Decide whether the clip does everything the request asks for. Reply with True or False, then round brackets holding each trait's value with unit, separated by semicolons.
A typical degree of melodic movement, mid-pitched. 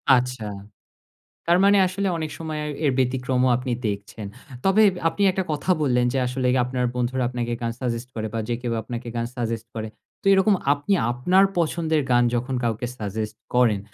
False (4.8 semitones; 125 Hz)